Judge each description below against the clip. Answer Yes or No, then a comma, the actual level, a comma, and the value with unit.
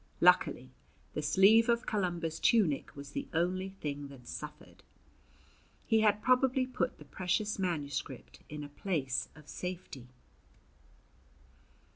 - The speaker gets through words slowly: Yes, slow, 120 wpm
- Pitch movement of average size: No, wide, 6.2 semitones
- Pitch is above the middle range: No, medium, 175 Hz